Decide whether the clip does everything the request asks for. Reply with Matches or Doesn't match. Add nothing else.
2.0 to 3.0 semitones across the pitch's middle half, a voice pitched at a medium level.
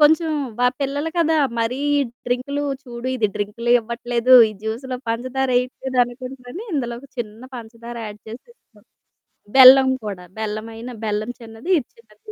Doesn't match